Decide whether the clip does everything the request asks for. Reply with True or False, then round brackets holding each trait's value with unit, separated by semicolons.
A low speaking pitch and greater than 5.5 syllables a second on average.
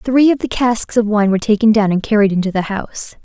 False (215 Hz; 6.2 syllables/s)